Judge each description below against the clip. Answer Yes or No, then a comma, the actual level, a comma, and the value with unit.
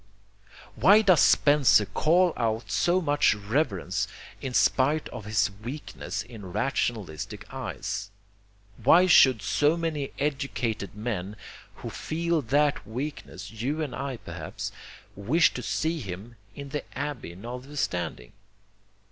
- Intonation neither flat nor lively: No, wide, 6.0 semitones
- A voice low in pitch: Yes, low, 130 Hz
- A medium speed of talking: No, slow, 120 wpm